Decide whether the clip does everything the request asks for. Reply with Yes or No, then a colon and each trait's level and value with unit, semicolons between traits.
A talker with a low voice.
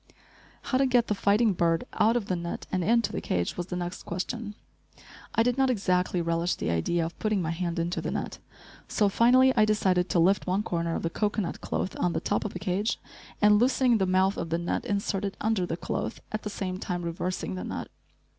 No: high, 190 Hz